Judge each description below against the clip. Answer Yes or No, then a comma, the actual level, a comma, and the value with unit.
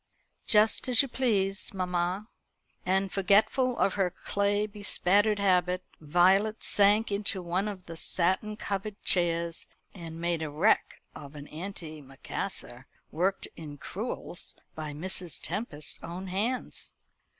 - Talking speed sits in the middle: No, slow, 125 wpm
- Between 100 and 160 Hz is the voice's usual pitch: No, high, 190 Hz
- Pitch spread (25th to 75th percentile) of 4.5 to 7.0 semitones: No, average, 3.3 semitones